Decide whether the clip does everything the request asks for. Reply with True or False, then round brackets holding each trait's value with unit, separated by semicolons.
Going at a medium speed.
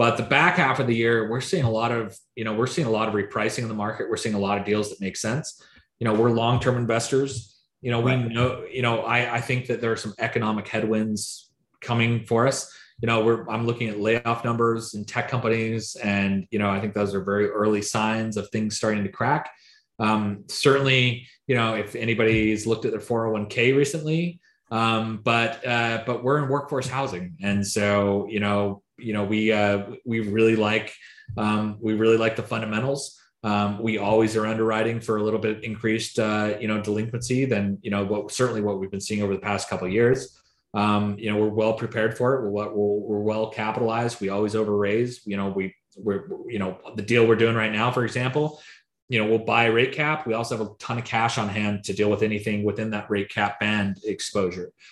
False (220 wpm)